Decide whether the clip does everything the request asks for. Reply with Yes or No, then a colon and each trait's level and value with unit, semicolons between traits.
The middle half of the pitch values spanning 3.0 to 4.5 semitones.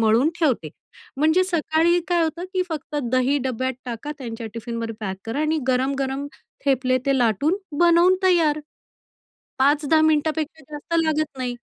Yes: average, 3.7 semitones